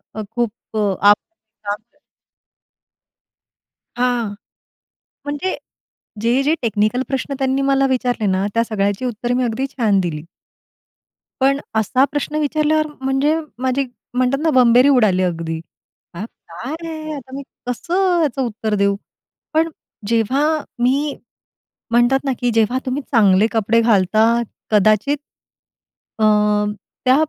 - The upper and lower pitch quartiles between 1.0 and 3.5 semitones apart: No, average, 4.3 semitones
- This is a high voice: Yes, high, 245 Hz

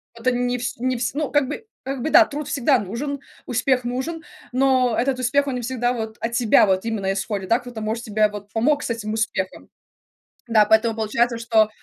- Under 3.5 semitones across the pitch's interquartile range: Yes, average, 2.9 semitones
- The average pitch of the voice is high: Yes, high, 240 Hz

